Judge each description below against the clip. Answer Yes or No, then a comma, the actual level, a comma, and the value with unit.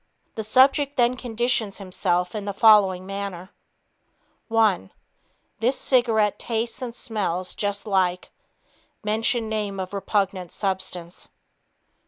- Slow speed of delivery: Yes, slow, 110 wpm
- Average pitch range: Yes, average, 3.3 semitones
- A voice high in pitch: Yes, high, 205 Hz